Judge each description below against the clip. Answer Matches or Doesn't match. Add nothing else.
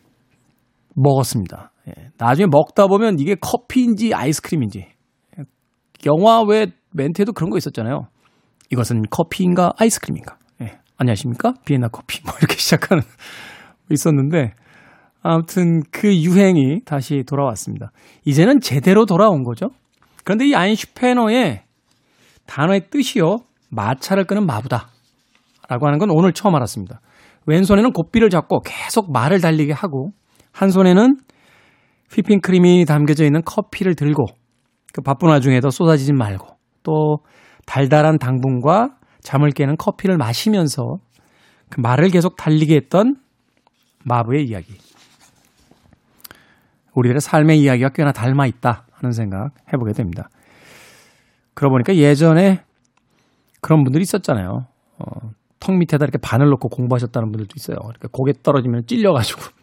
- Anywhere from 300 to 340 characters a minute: Matches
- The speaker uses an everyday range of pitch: Doesn't match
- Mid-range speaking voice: Matches